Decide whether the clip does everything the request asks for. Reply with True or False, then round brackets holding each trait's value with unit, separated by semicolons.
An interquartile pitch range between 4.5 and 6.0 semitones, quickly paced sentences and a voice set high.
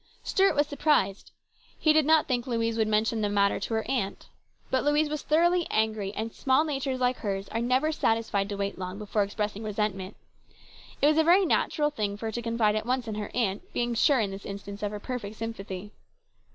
True (4.8 semitones; 215 wpm; 225 Hz)